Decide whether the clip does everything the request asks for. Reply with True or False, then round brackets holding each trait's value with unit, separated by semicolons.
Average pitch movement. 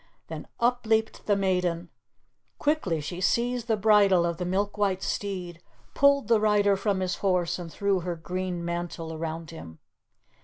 True (3.4 semitones)